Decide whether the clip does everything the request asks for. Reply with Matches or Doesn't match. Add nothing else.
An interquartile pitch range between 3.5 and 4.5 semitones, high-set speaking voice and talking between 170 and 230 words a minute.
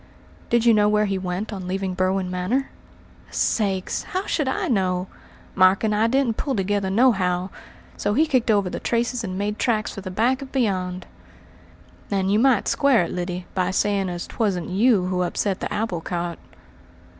Matches